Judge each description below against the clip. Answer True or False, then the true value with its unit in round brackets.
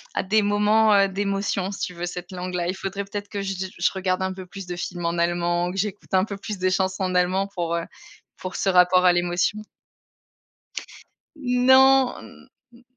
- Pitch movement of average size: False (2.2 semitones)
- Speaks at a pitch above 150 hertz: True (190 Hz)